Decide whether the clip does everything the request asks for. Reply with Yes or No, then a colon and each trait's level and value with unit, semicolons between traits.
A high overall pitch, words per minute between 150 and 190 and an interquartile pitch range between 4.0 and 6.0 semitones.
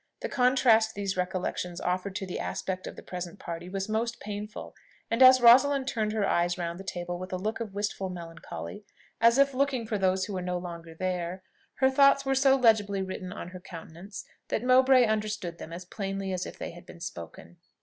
No: high, 195 Hz; fast, 205 wpm; average, 4.3 semitones